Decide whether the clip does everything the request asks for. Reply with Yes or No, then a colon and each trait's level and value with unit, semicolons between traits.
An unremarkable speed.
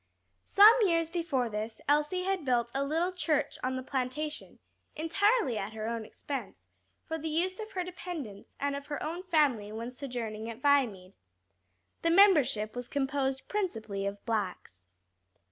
Yes: average, 155 wpm